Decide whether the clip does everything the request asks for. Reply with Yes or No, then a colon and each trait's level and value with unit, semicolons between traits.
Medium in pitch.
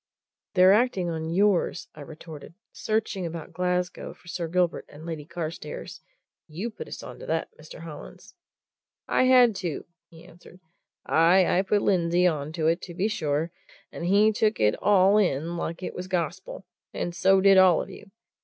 Yes: medium, 180 Hz